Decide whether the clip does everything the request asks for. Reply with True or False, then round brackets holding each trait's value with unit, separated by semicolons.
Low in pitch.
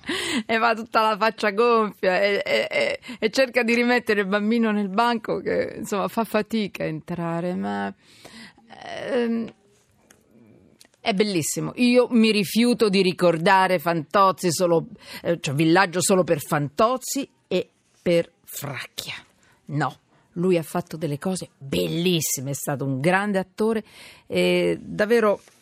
False (200 Hz)